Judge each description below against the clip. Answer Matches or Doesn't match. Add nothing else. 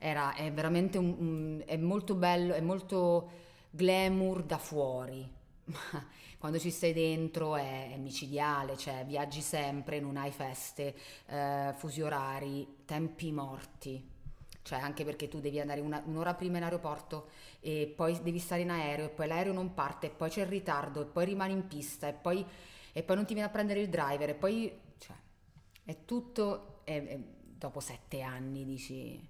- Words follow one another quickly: Matches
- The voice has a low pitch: Doesn't match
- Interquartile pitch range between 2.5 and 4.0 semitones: Matches